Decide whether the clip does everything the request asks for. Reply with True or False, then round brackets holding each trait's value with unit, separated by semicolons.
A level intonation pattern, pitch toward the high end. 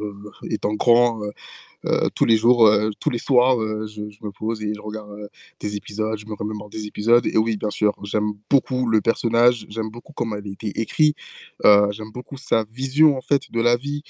False (2.3 semitones; 110 Hz)